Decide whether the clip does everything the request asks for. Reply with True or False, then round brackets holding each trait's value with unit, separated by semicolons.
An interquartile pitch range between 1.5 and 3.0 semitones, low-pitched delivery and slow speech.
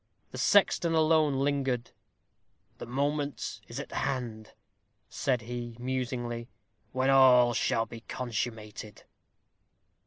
True (2.7 semitones; 125 Hz; 100 wpm)